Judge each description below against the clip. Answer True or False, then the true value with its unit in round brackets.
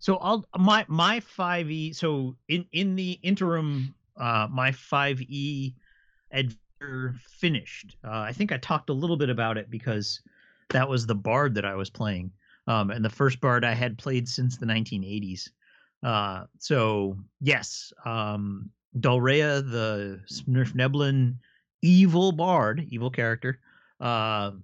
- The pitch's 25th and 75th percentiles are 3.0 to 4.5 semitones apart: False (5.4 semitones)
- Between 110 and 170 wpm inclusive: True (150 wpm)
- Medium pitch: False (130 Hz)